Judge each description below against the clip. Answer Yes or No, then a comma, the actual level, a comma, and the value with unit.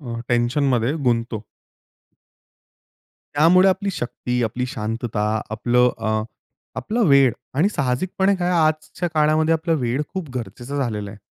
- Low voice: Yes, low, 125 Hz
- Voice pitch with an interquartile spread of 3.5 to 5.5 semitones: Yes, average, 5.2 semitones